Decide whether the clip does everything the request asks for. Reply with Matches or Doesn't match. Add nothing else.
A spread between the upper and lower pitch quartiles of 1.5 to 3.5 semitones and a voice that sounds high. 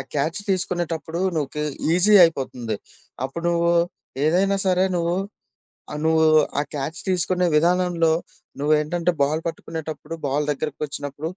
Doesn't match